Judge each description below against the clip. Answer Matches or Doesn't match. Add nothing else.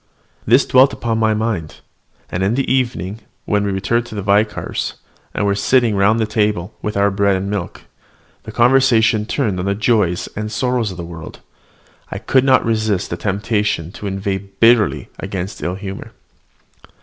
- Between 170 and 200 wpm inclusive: Matches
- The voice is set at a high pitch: Doesn't match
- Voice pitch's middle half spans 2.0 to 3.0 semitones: Matches